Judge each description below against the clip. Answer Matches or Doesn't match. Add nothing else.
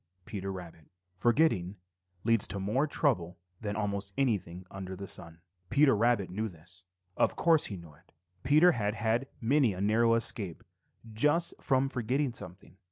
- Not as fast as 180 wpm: Matches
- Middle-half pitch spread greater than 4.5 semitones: Matches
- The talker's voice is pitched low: Matches